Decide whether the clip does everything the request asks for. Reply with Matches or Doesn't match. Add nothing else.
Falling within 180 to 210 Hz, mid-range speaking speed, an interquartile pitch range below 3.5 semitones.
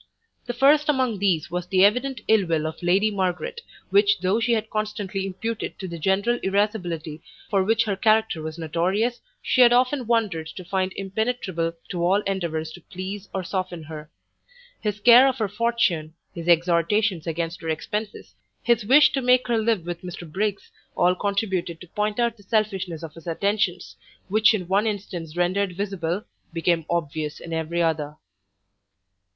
Doesn't match